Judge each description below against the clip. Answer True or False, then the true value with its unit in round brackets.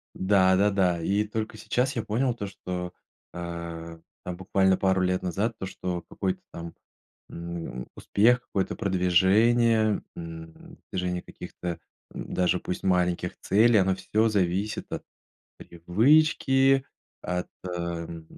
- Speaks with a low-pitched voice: True (95 Hz)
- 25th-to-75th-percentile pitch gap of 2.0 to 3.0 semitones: False (3.6 semitones)